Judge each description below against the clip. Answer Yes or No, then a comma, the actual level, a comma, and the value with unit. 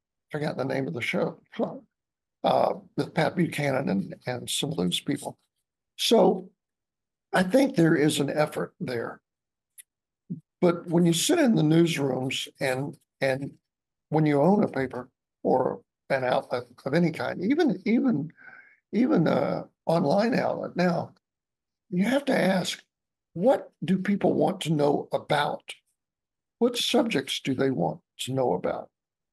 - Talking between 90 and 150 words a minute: Yes, average, 145 wpm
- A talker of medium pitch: Yes, medium, 165 Hz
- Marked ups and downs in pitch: Yes, wide, 6.3 semitones